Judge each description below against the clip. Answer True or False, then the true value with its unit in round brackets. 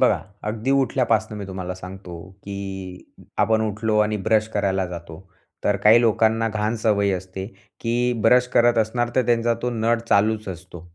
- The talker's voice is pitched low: True (105 Hz)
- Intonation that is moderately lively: True (3.2 semitones)